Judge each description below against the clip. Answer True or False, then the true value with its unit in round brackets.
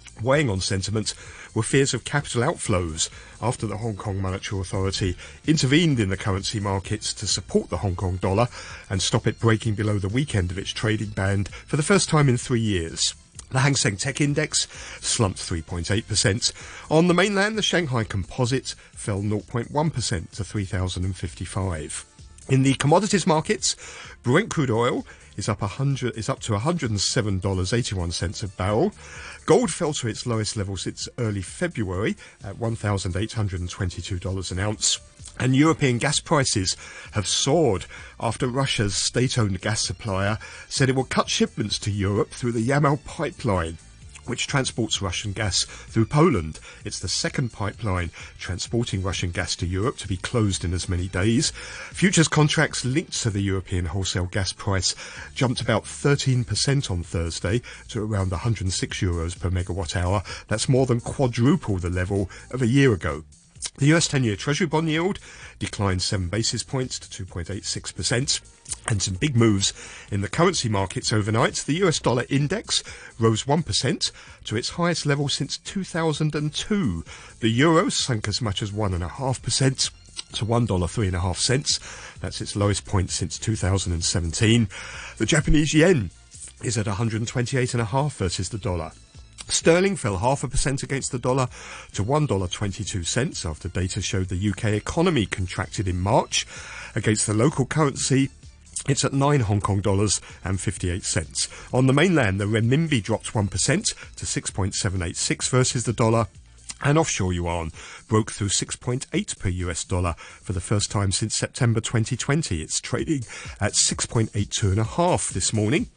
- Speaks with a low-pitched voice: True (110 Hz)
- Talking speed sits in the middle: True (165 wpm)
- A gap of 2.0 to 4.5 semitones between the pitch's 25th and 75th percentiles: False (5.5 semitones)